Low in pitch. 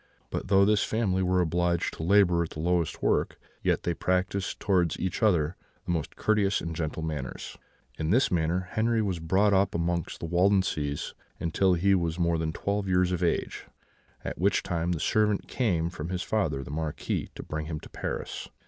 Yes: very low, 90 Hz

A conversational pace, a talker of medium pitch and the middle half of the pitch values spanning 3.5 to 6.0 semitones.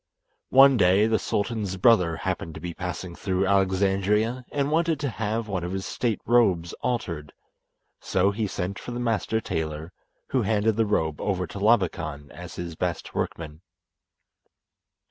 No: average, 155 wpm; low, 100 Hz; average, 4.2 semitones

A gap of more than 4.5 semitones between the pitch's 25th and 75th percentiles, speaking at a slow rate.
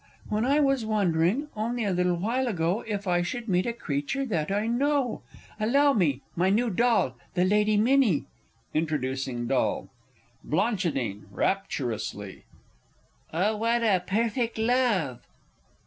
Yes: wide, 5.6 semitones; slow, 130 wpm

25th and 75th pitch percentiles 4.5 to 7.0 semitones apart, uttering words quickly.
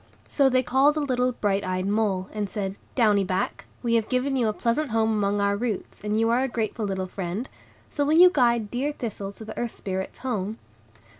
No: average, 3.8 semitones; fast, 215 wpm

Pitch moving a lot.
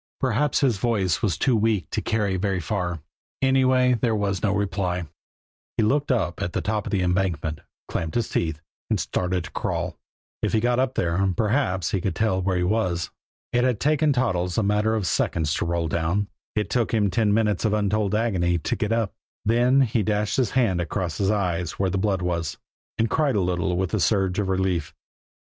No: average, 4.0 semitones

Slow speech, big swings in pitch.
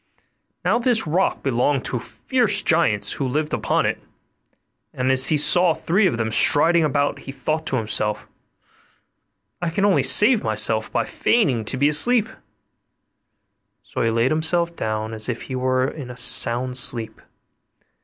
No: average, 155 wpm; wide, 6.4 semitones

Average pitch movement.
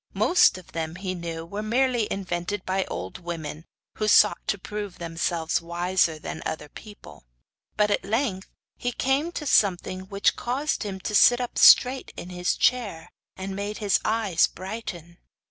Yes: average, 3.9 semitones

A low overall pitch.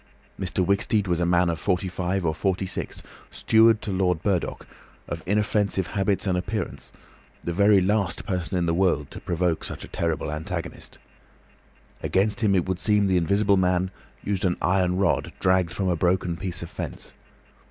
Yes: very low, 95 Hz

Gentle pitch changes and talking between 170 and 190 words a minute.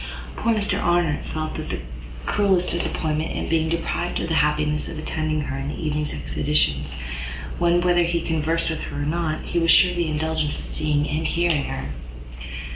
Yes: narrow, 2.3 semitones; average, 185 wpm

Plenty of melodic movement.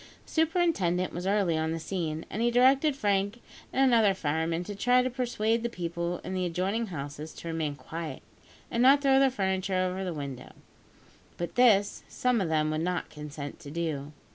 Yes: wide, 6.5 semitones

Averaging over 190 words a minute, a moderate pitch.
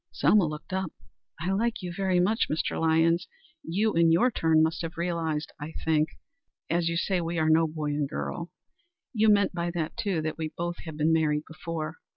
Yes: average, 200 wpm; medium, 165 Hz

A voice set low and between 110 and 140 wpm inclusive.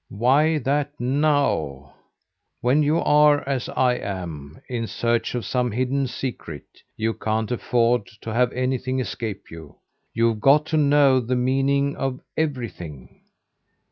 Yes: low, 125 Hz; slow, 135 wpm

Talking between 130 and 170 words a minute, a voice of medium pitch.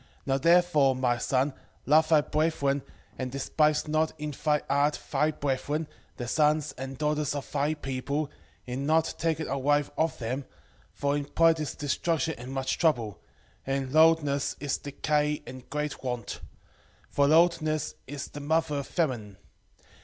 Yes: average, 160 wpm; medium, 145 Hz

